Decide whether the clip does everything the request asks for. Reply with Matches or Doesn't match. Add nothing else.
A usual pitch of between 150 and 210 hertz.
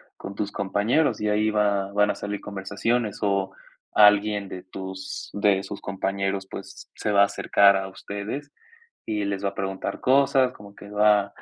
Doesn't match